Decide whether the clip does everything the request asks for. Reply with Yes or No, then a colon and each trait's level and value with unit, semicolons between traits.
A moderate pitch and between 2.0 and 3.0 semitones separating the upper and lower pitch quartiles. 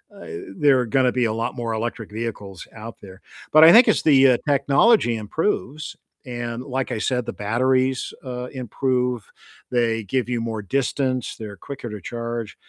No: low, 125 Hz; average, 2.7 semitones